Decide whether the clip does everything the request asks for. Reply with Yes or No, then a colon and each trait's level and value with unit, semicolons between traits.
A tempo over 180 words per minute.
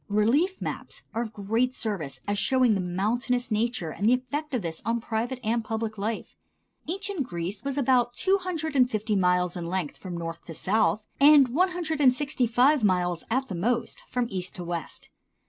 Yes: average, 195 wpm